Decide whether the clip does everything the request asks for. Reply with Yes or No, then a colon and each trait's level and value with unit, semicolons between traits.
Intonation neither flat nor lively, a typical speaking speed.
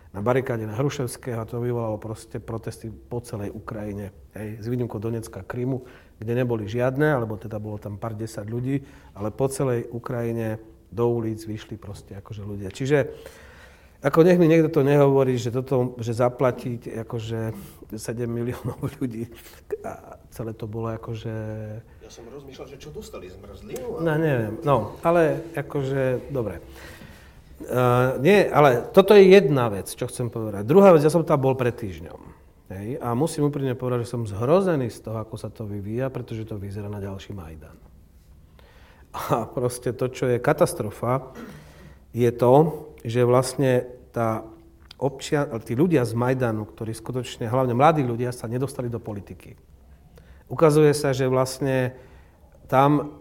Yes: average, 3.4 semitones; average, 155 wpm